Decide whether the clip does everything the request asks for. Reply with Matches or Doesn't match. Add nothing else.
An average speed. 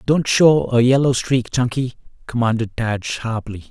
Matches